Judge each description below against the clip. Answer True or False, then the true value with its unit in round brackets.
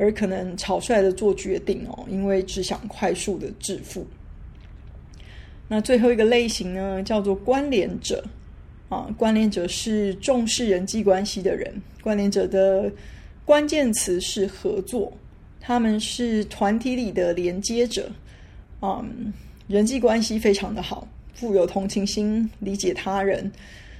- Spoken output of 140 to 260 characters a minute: True (210 characters per minute)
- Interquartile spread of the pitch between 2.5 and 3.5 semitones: True (2.8 semitones)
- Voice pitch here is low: False (205 Hz)